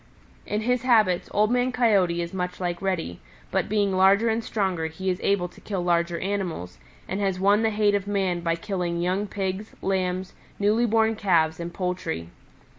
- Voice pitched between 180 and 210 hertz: Yes, high, 190 Hz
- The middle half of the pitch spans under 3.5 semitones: Yes, average, 2.9 semitones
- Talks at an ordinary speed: Yes, average, 185 wpm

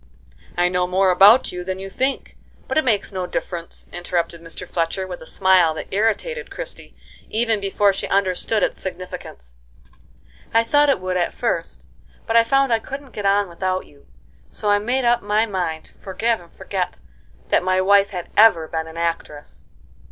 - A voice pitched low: No, high, 190 Hz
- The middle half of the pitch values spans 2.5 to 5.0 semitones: Yes, average, 4.0 semitones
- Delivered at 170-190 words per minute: Yes, average, 180 wpm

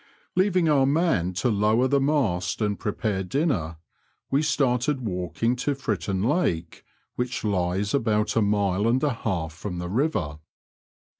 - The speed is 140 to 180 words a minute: Yes, average, 145 wpm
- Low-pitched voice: Yes, low, 110 Hz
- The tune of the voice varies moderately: No, wide, 6.7 semitones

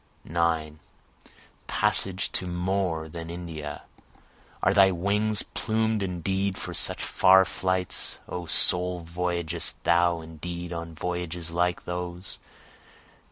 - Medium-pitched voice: No, very low, 90 Hz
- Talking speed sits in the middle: No, slow, 110 wpm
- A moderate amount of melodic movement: No, narrow, 1.8 semitones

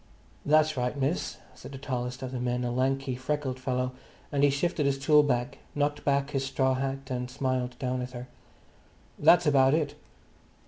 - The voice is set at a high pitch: No, low, 135 Hz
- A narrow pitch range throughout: Yes, narrow, 2.1 semitones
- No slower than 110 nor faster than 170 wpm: No, average, 180 wpm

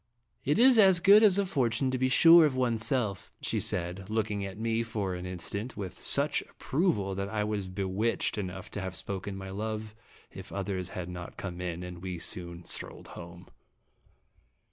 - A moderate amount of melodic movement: Yes, average, 4.6 semitones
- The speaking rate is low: No, average, 190 wpm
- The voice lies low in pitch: Yes, low, 100 Hz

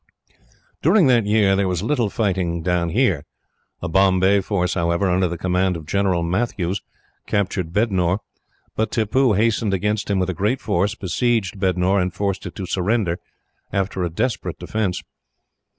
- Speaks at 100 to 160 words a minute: Yes, average, 155 wpm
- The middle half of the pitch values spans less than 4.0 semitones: Yes, average, 2.9 semitones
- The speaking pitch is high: No, very low, 95 Hz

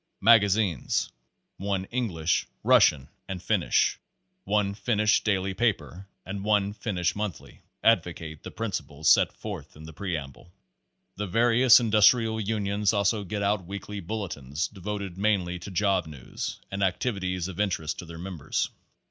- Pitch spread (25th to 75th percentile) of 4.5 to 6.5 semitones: No, average, 3.2 semitones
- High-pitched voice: No, low, 100 Hz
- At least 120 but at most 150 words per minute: Yes, average, 140 wpm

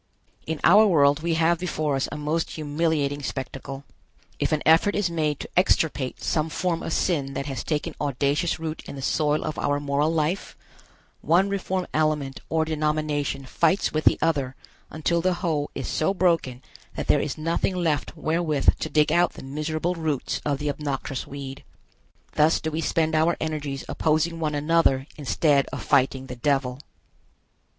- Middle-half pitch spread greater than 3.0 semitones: No, narrow, 2.6 semitones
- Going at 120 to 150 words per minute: No, average, 170 wpm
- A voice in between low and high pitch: Yes, medium, 155 Hz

